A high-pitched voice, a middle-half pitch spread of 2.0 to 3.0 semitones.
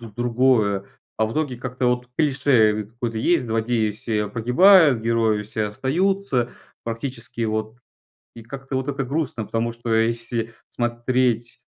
No: low, 120 Hz; average, 2.7 semitones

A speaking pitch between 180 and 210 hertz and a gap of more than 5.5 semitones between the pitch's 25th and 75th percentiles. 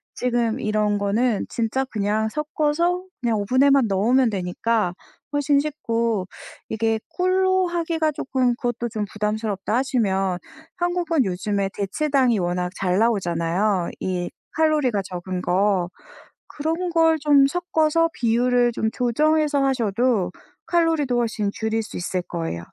No: high, 235 Hz; wide, 6.5 semitones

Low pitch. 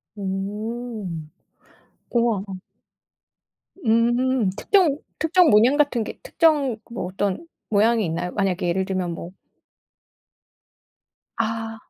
No: high, 225 Hz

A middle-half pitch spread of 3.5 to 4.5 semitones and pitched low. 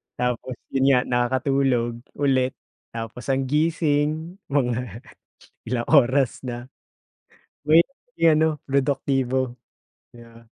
No: average, 2.9 semitones; low, 130 Hz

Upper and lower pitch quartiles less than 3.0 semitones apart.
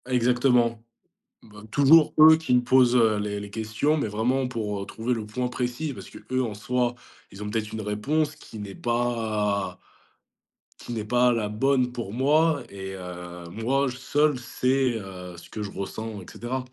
No: average, 3.6 semitones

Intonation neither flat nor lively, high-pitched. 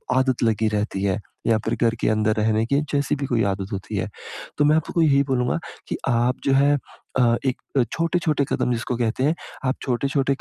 No: average, 3.9 semitones; low, 125 Hz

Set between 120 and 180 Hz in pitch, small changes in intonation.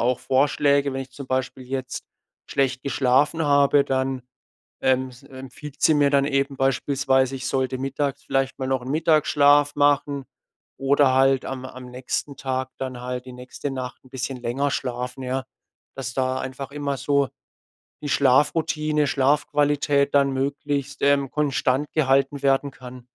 Yes: low, 135 Hz; narrow, 1.6 semitones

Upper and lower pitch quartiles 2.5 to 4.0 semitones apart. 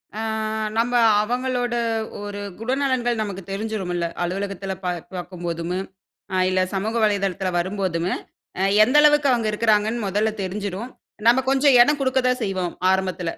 No: average, 4.4 semitones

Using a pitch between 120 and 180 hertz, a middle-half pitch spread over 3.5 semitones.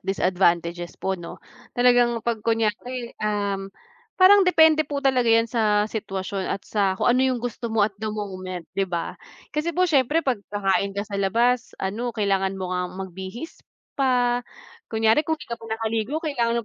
No: high, 220 Hz; average, 4.1 semitones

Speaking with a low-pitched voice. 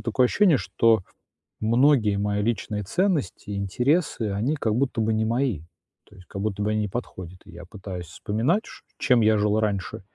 Yes: low, 110 Hz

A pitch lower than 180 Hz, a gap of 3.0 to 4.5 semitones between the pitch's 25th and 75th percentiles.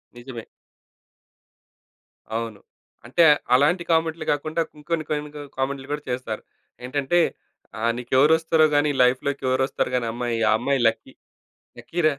Yes: medium, 140 Hz; average, 4.0 semitones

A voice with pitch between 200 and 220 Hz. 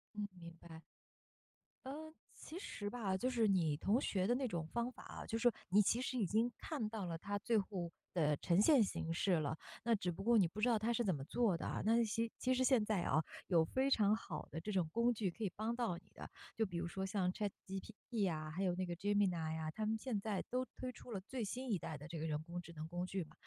Yes: high, 205 Hz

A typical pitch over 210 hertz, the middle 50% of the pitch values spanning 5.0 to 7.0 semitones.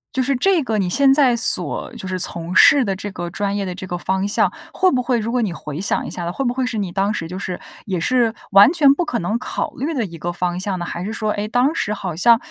No: high, 205 Hz; wide, 5.4 semitones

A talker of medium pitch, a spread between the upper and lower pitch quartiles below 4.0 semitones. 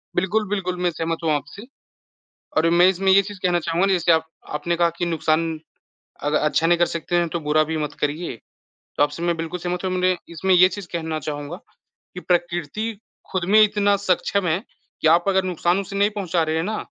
Yes: medium, 175 Hz; narrow, 2.6 semitones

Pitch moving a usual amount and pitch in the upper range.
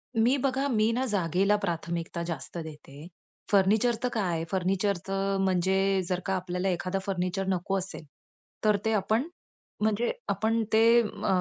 Yes: average, 3.4 semitones; high, 195 Hz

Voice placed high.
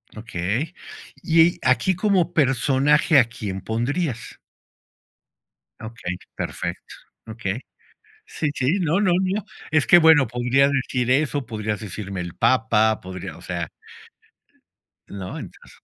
No: low, 130 Hz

